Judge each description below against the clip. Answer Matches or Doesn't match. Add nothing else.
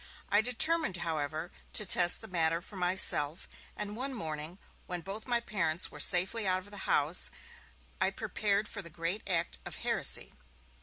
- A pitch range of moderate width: Matches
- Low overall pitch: Doesn't match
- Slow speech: Doesn't match